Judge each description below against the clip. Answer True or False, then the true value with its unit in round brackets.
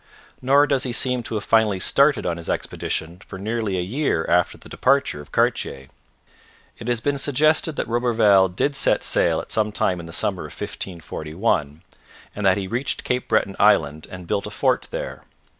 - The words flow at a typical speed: True (190 wpm)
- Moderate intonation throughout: False (6.2 semitones)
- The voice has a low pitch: True (105 Hz)